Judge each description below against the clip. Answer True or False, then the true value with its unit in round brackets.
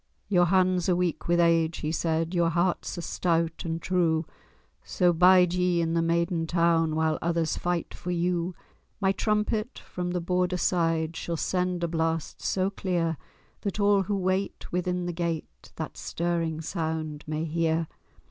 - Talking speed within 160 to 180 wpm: True (165 wpm)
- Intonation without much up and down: True (1.7 semitones)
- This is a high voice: False (170 Hz)